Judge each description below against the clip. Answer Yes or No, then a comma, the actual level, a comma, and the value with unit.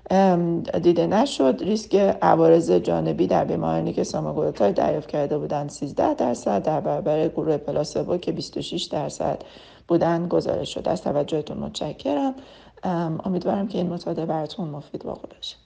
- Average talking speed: Yes, average, 135 wpm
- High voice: No, medium, 170 Hz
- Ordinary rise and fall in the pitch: Yes, average, 4.2 semitones